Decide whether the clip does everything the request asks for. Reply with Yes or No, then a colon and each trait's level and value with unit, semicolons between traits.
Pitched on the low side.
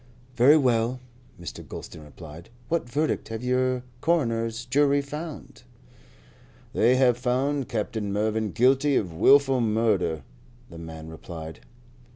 Yes: low, 120 Hz